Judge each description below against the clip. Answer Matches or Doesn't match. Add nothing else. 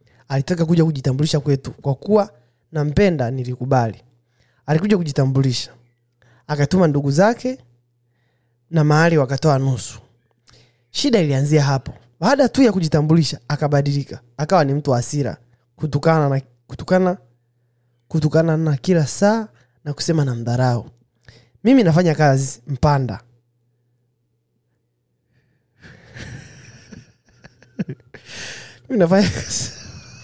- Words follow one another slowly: Matches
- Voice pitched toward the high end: Doesn't match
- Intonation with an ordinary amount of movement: Matches